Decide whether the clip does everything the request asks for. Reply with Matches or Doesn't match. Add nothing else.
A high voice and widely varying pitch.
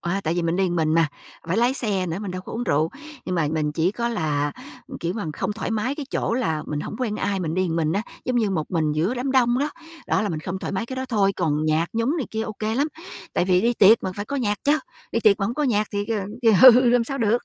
Matches